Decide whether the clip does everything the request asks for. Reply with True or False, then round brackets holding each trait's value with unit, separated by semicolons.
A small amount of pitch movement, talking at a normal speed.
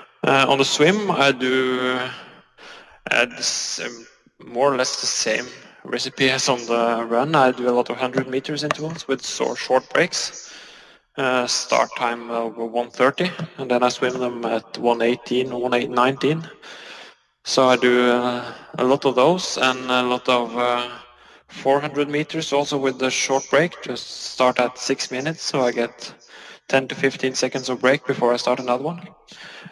True (1.9 semitones; 165 wpm)